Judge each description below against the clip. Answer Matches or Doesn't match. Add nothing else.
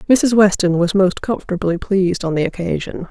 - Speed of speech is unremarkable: Matches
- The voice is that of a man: Doesn't match